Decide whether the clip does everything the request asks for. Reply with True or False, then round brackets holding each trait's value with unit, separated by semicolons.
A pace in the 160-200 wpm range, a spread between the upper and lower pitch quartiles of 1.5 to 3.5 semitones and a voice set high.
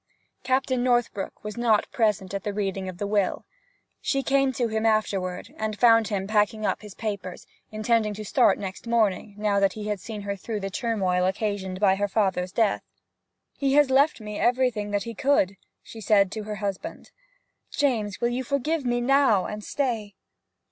True (185 wpm; 3.2 semitones; 215 Hz)